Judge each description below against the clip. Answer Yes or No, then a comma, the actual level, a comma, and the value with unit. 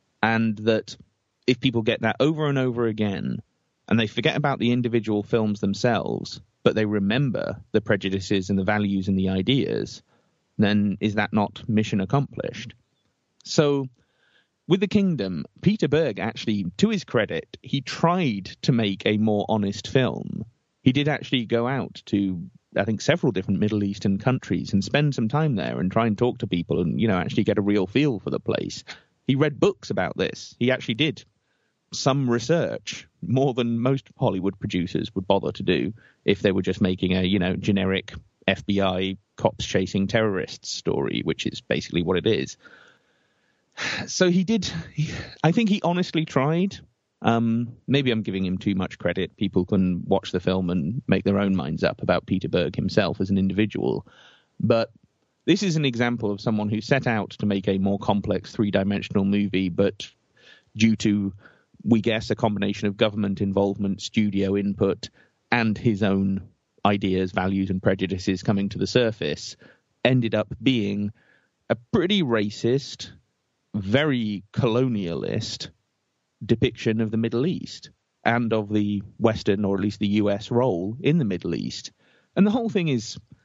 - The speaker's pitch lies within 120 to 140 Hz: No, low, 110 Hz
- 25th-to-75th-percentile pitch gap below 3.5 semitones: No, average, 4.4 semitones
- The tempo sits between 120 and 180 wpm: Yes, average, 170 wpm